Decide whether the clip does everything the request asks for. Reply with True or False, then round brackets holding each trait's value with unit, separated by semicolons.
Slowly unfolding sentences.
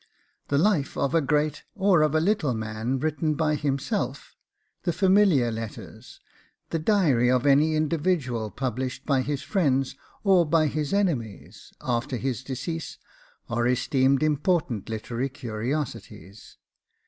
True (130 wpm)